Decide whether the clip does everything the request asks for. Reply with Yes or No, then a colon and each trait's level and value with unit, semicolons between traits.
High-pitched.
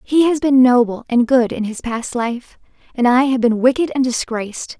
Yes: very high, 250 Hz